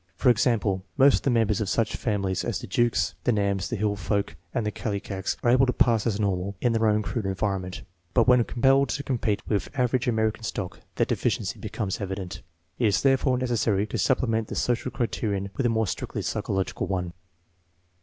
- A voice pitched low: Yes, low, 110 Hz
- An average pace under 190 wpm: No, average, 195 wpm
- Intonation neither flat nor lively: Yes, average, 3.5 semitones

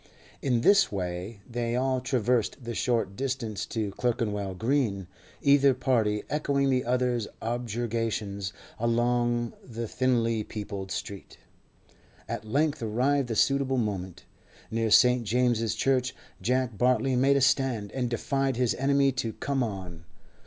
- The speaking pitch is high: No, low, 120 Hz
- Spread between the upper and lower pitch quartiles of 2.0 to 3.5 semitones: Yes, average, 3.2 semitones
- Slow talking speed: Yes, slow, 130 wpm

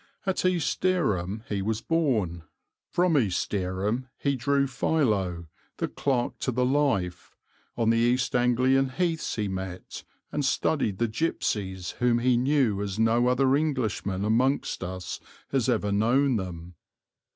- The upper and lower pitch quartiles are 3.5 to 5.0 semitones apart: No, wide, 5.4 semitones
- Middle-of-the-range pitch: No, low, 120 Hz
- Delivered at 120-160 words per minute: Yes, average, 140 wpm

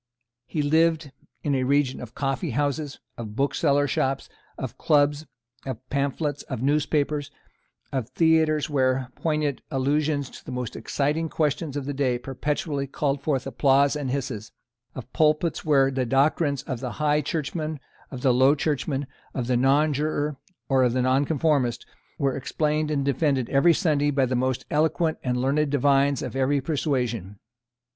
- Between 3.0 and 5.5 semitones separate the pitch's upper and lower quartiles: No, narrow, 2.4 semitones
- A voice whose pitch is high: No, medium, 140 Hz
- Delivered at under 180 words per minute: Yes, average, 150 wpm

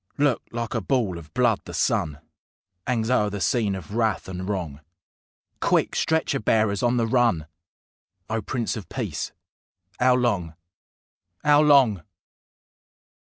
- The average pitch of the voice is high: No, low, 110 Hz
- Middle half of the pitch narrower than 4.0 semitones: No, average, 4.5 semitones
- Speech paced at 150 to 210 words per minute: No, slow, 135 wpm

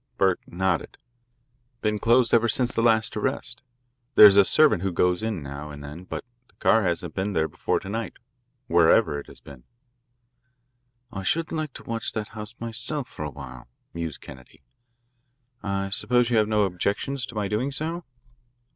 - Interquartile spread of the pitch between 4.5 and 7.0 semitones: Yes, average, 5.1 semitones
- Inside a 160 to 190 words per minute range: Yes, average, 175 wpm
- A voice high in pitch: No, low, 105 Hz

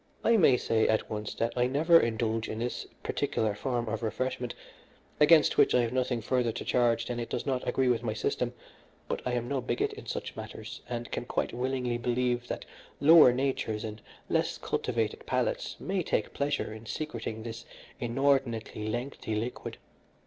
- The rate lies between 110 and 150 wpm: No, average, 180 wpm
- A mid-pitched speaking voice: No, low, 120 Hz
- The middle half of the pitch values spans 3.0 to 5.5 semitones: No, narrow, 2.4 semitones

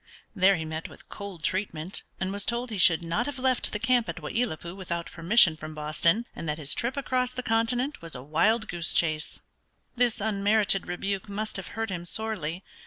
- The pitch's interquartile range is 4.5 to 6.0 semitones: Yes, average, 5.3 semitones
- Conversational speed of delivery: No, fast, 210 wpm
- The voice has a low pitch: No, high, 195 Hz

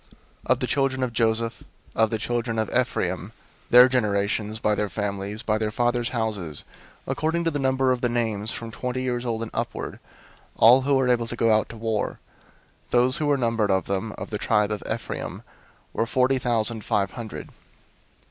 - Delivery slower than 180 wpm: No, average, 195 wpm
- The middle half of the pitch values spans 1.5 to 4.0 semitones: Yes, average, 2.7 semitones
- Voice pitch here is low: Yes, low, 115 Hz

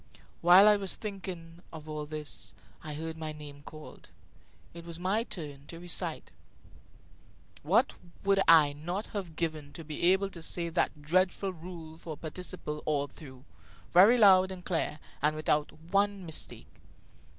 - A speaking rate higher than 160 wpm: No, average, 155 wpm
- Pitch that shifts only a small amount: No, average, 3.4 semitones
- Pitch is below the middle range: No, medium, 165 Hz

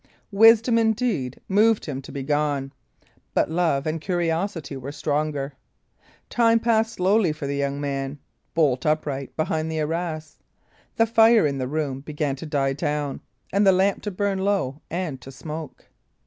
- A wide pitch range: Yes, wide, 5.8 semitones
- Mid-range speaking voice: Yes, medium, 155 Hz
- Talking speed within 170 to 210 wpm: No, average, 160 wpm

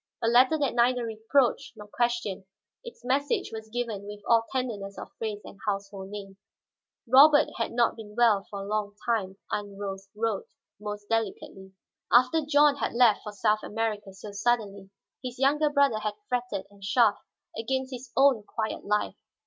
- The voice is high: Yes, high, 225 Hz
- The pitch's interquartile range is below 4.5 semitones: Yes, average, 3.5 semitones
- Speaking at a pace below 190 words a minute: Yes, average, 165 wpm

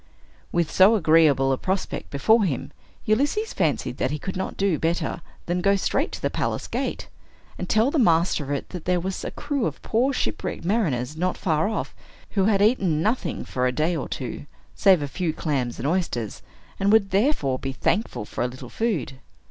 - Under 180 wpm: No, average, 195 wpm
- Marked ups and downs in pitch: Yes, wide, 6.2 semitones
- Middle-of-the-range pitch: Yes, medium, 175 Hz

